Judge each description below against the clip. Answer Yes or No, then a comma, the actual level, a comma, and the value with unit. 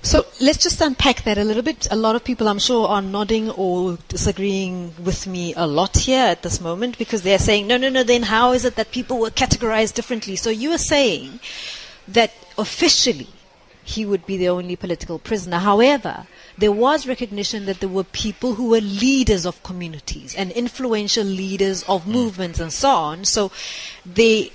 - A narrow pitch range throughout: No, average, 4.2 semitones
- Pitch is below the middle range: No, high, 215 Hz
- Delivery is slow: No, average, 190 wpm